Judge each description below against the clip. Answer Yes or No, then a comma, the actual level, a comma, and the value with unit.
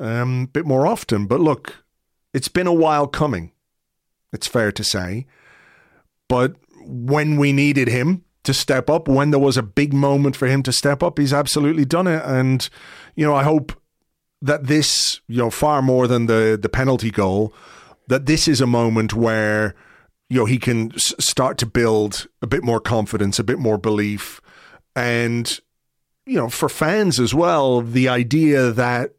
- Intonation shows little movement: No, average, 3.9 semitones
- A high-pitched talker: No, low, 130 Hz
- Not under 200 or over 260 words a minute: No, average, 180 wpm